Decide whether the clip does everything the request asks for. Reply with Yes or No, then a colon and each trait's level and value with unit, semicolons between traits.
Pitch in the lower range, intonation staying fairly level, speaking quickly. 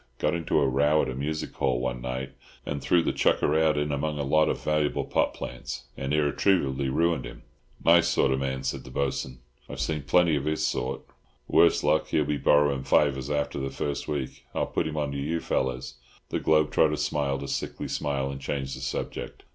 Yes: very low, 70 Hz; narrow, 2.3 semitones; fast, 210 wpm